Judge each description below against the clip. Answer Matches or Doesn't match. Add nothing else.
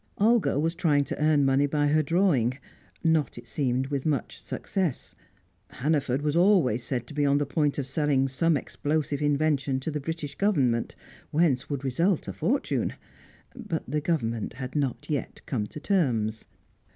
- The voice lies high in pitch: Doesn't match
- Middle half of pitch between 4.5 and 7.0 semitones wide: Doesn't match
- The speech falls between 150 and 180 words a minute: Matches